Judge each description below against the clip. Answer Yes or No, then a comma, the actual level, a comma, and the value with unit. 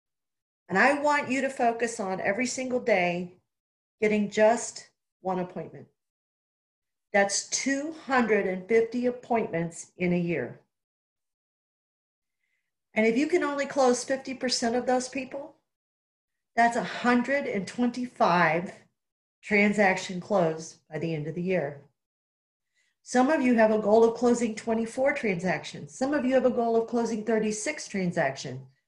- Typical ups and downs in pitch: No, wide, 5.9 semitones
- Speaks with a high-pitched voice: Yes, high, 225 Hz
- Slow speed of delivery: Yes, slow, 125 wpm